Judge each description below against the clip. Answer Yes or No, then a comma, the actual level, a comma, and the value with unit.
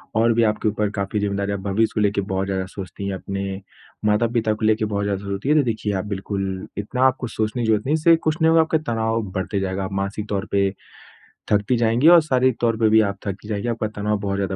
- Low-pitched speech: Yes, low, 105 Hz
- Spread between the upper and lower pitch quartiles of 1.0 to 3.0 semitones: Yes, average, 2.7 semitones